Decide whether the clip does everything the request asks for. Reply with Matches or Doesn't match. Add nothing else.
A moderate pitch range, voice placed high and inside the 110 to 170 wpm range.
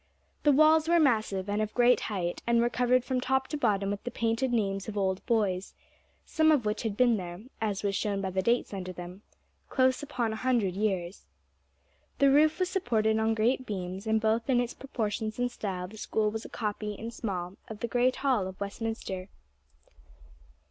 Doesn't match